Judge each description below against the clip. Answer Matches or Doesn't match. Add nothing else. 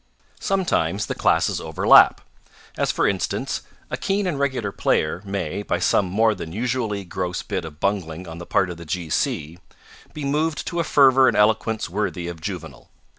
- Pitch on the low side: Matches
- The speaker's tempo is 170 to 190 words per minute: Matches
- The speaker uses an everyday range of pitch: Doesn't match